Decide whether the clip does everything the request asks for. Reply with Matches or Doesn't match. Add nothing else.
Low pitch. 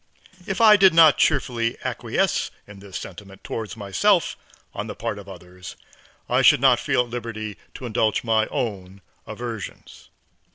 Matches